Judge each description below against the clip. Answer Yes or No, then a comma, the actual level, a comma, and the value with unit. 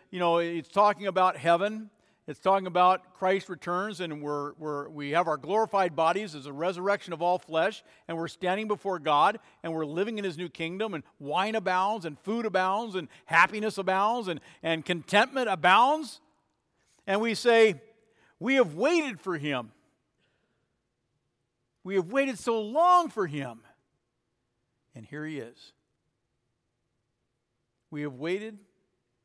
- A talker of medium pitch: Yes, medium, 180 Hz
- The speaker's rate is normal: Yes, average, 150 wpm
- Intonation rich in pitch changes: Yes, wide, 5.8 semitones